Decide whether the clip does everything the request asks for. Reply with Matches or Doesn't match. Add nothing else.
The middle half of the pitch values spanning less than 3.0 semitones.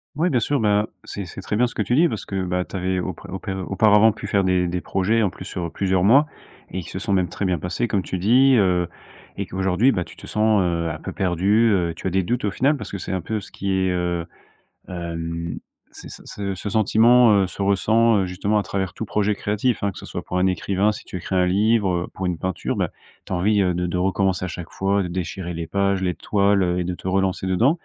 Matches